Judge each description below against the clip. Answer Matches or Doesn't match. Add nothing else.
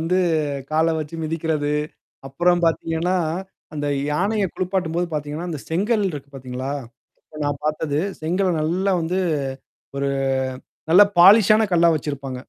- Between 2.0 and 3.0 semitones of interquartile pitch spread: Doesn't match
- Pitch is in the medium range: Matches